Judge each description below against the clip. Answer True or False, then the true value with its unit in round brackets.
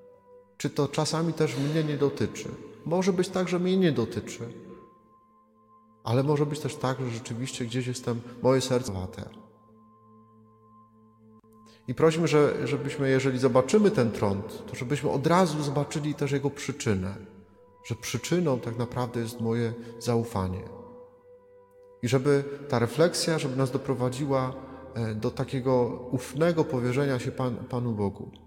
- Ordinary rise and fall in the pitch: True (4.2 semitones)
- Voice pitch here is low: True (130 Hz)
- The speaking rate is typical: True (135 wpm)